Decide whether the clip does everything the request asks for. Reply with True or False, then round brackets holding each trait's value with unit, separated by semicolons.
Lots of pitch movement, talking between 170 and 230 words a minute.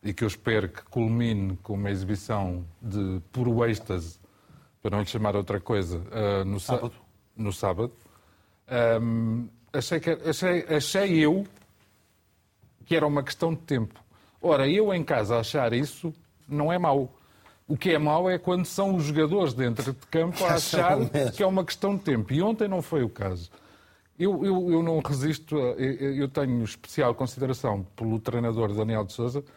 True (6.8 semitones; 175 wpm)